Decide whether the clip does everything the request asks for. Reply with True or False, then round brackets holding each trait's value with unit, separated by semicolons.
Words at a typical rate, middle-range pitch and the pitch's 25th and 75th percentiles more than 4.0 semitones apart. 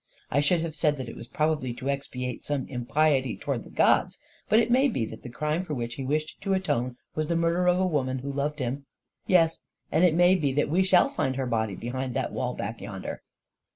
False (245 wpm; 145 Hz; 4.6 semitones)